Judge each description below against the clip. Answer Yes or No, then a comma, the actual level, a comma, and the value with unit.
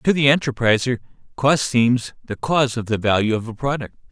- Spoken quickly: No, average, 190 wpm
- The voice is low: Yes, low, 125 Hz